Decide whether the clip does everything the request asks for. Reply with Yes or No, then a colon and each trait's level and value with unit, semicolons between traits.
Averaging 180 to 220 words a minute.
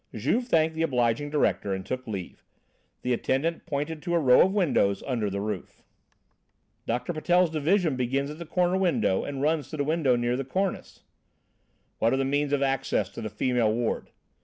Yes: average, 185 wpm